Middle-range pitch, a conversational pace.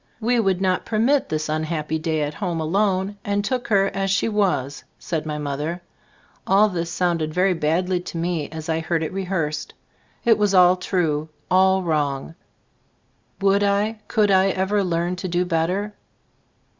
Yes: medium, 180 Hz; average, 170 wpm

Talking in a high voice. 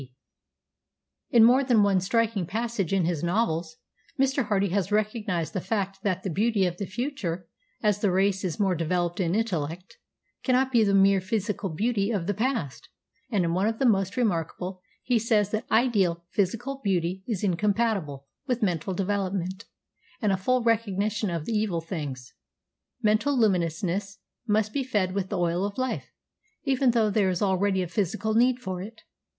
Yes: high, 200 Hz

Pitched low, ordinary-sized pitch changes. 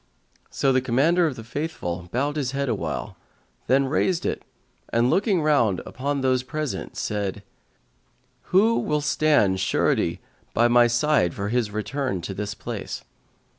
No: low, 130 Hz; wide, 5.8 semitones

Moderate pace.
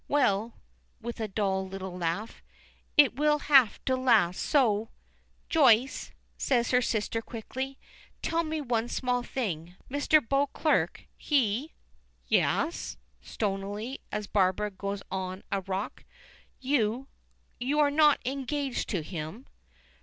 No: slow, 125 wpm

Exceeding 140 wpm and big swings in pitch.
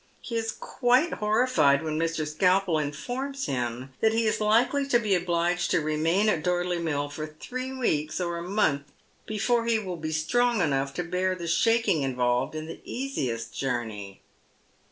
Yes: average, 170 wpm; wide, 6.9 semitones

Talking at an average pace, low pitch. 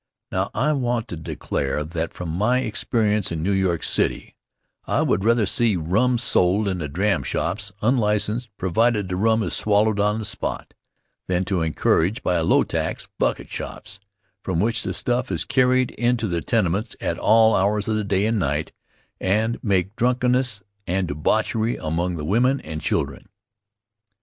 Yes: average, 170 wpm; low, 105 Hz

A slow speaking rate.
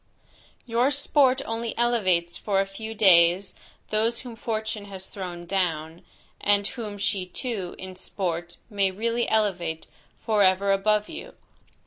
Yes: slow, 130 wpm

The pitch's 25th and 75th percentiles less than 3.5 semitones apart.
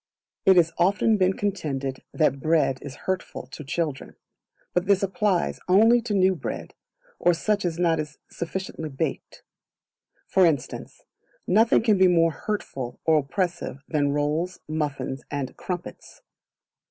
No: average, 4.4 semitones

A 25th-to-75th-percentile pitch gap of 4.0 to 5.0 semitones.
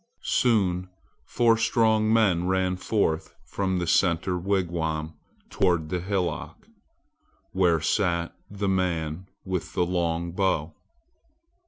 No: narrow, 2.5 semitones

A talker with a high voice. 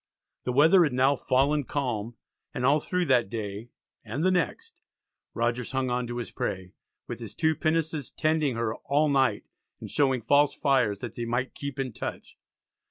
No: low, 130 Hz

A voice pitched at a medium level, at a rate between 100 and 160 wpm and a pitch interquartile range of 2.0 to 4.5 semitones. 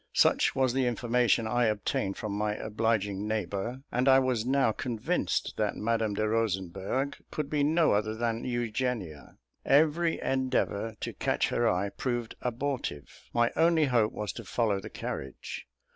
No: low, 115 Hz; average, 155 wpm; average, 3.5 semitones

